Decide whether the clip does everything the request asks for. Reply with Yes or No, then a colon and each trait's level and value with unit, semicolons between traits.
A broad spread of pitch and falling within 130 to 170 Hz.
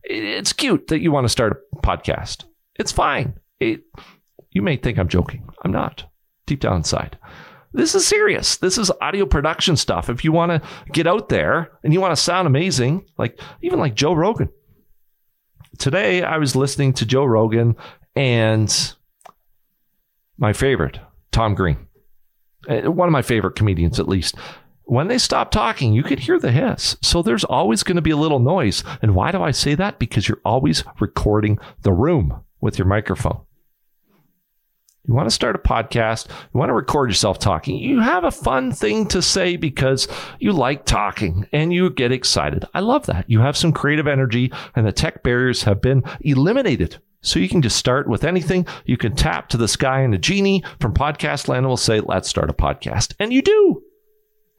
Yes: wide, 7.9 semitones; low, 135 Hz